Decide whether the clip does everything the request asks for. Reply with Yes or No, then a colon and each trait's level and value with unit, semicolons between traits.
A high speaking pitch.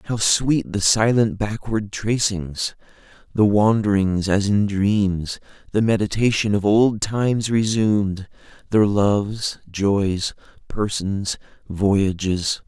No: low, 105 Hz